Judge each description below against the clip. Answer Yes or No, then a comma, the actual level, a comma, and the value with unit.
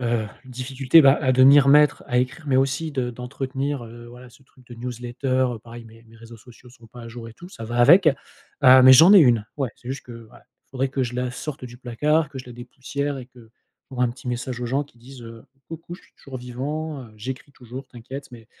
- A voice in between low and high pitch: No, low, 125 Hz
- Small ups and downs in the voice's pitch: Yes, narrow, 2.3 semitones